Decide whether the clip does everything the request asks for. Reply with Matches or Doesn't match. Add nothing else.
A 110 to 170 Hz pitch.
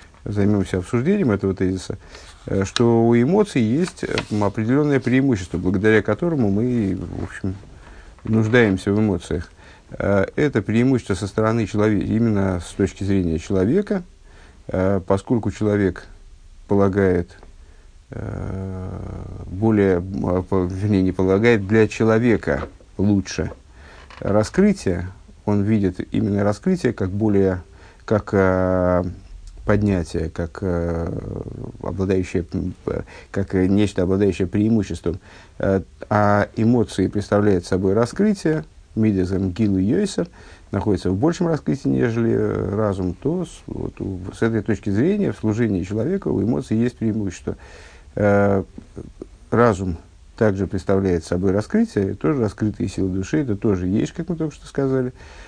Doesn't match